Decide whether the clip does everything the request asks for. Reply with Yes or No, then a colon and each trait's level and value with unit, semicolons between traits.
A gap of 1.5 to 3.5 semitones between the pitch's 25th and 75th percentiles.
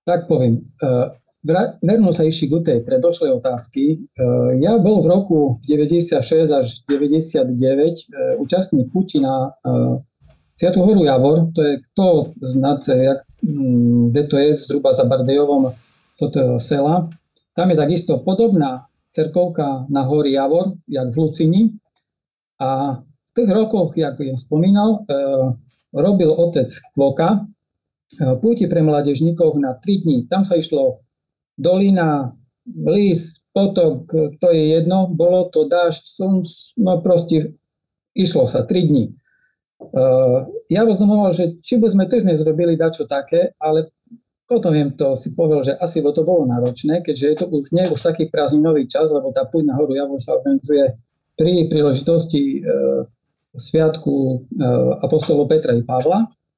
No: average, 4.3 semitones